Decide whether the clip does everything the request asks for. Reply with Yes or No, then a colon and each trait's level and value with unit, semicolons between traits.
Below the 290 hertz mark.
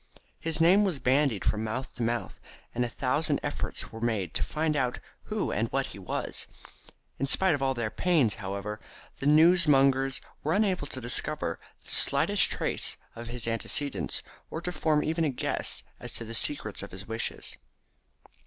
Yes: low, 135 Hz